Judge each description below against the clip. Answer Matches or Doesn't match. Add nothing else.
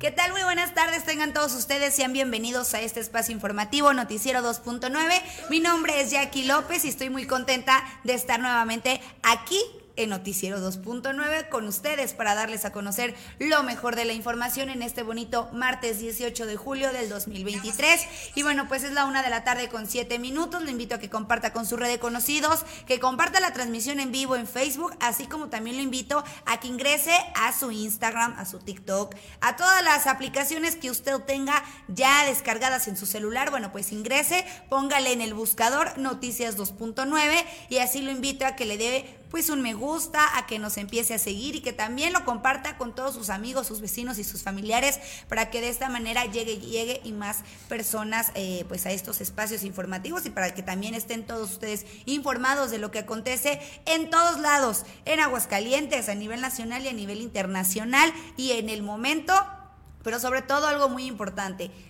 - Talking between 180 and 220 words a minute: Matches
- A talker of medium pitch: Doesn't match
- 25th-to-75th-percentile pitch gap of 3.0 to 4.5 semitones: Matches